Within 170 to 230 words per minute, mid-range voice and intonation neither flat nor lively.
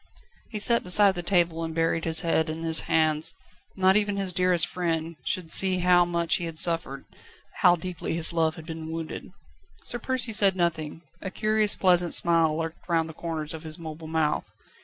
No: average, 190 wpm; medium, 170 Hz; narrow, 2.2 semitones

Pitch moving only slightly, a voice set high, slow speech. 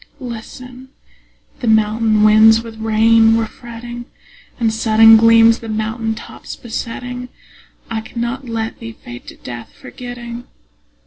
Yes: narrow, 1.3 semitones; high, 225 Hz; slow, 125 wpm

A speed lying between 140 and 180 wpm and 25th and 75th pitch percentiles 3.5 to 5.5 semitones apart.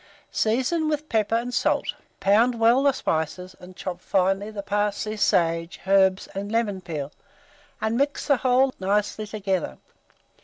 Yes: average, 145 wpm; average, 3.9 semitones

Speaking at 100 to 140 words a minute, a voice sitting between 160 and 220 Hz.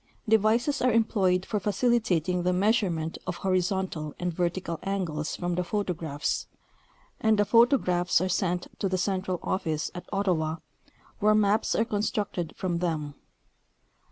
Yes: slow, 135 wpm; medium, 185 Hz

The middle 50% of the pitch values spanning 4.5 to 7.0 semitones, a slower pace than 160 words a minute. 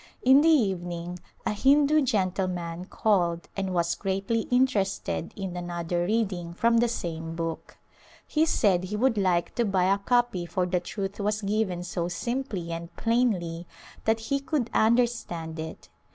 Yes: average, 4.9 semitones; average, 150 wpm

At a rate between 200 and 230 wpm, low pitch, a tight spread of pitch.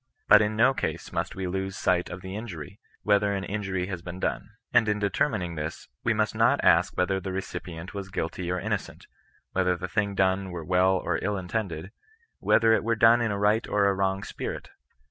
Yes: fast, 205 wpm; very low, 95 Hz; narrow, 2.3 semitones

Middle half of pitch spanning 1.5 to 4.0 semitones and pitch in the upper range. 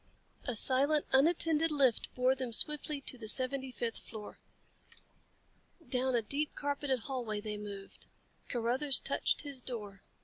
Yes: average, 3.7 semitones; very high, 255 Hz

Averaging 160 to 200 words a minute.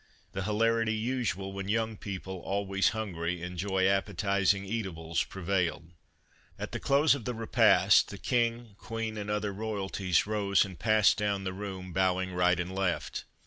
No: average, 150 wpm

